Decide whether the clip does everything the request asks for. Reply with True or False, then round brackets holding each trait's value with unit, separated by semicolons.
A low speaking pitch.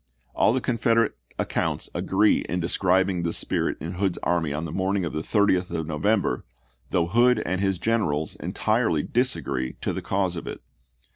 True (95 Hz)